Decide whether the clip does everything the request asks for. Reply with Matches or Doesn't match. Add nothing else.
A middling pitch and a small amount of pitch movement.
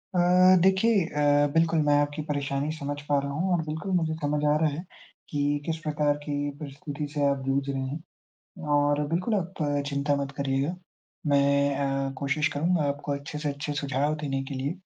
Matches